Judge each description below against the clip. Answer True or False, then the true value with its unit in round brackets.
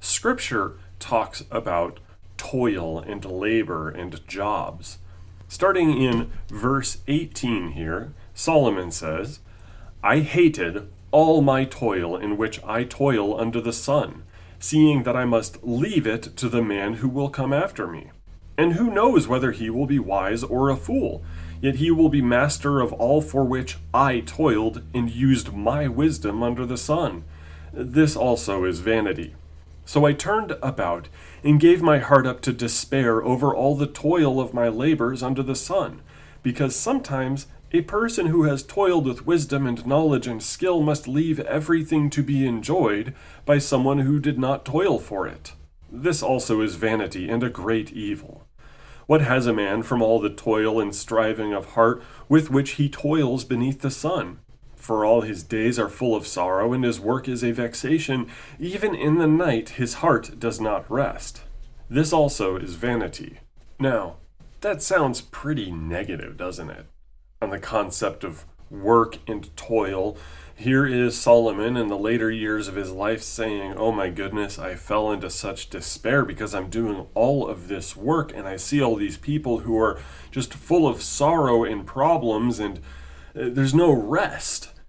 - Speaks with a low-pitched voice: True (115 Hz)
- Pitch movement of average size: False (5.9 semitones)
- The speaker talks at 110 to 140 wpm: False (165 wpm)